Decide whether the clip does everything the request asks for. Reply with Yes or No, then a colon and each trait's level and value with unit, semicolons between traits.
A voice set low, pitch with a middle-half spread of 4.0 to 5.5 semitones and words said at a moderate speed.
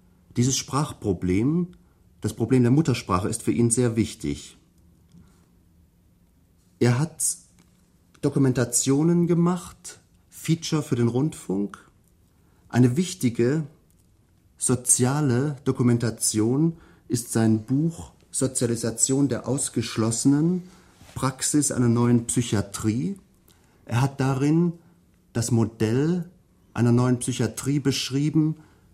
No: low, 120 Hz; average, 4.9 semitones; slow, 85 wpm